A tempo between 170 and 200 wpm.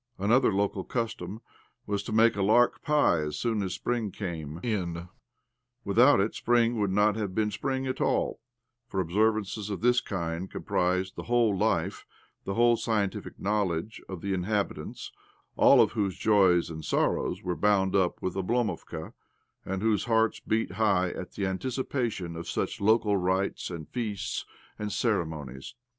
No: average, 155 wpm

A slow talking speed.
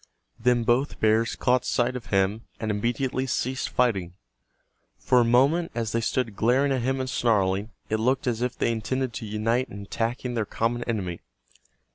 No: average, 175 wpm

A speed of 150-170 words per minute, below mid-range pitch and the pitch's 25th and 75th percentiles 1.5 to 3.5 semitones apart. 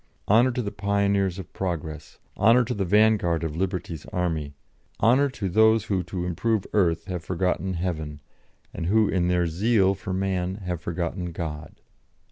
Yes: average, 160 wpm; very low, 95 Hz; average, 3.0 semitones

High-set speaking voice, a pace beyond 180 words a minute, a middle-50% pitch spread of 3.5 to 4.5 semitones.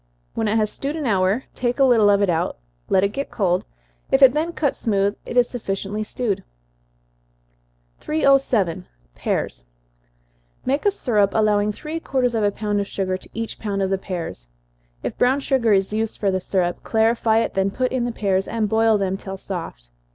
Yes: high, 215 Hz; average, 190 wpm; average, 4.1 semitones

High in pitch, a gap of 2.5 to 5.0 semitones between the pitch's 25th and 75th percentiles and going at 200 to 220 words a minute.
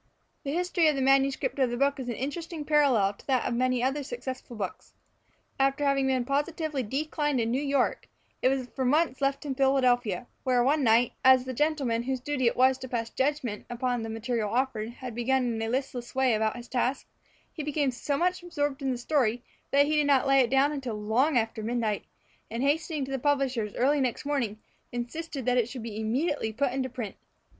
Yes: very high, 260 Hz; average, 2.9 semitones; fast, 205 wpm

